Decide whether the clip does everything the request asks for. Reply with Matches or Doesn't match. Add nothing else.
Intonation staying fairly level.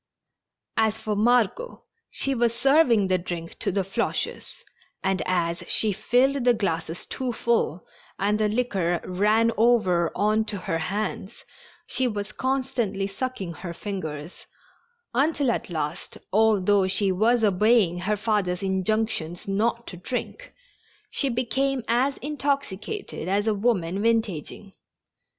Doesn't match